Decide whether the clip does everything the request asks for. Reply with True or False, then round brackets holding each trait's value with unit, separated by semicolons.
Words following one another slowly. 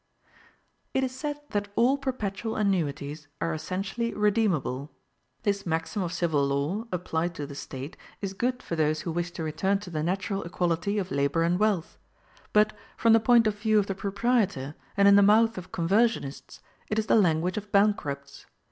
False (180 wpm)